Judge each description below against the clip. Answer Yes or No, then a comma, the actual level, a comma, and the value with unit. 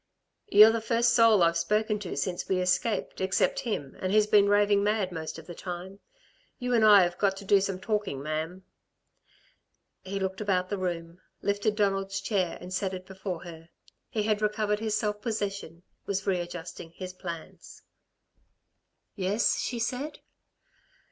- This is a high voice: Yes, high, 195 Hz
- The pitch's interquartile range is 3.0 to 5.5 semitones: No, narrow, 2.6 semitones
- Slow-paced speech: No, average, 160 wpm